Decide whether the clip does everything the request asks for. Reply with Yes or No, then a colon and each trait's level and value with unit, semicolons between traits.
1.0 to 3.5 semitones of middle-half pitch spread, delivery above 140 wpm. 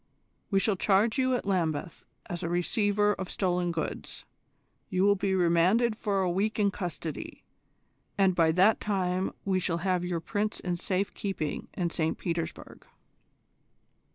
Yes: average, 2.8 semitones; average, 155 wpm